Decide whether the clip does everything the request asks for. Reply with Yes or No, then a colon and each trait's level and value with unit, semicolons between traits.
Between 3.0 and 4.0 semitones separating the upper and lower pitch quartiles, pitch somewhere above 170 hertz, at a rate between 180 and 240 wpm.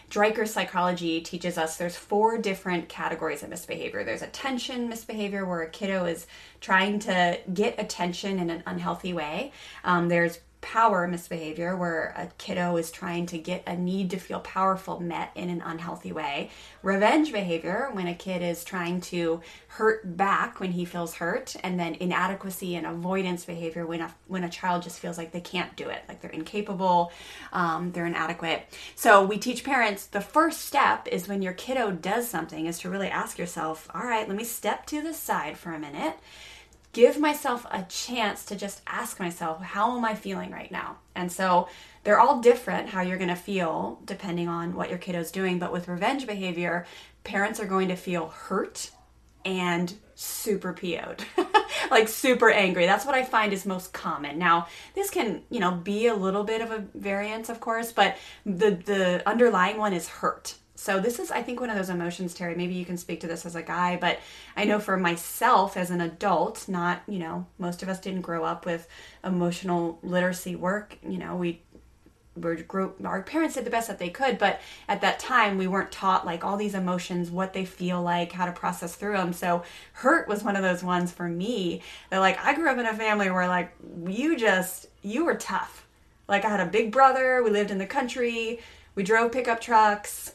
Yes: average, 3.4 semitones; medium, 185 Hz; average, 200 wpm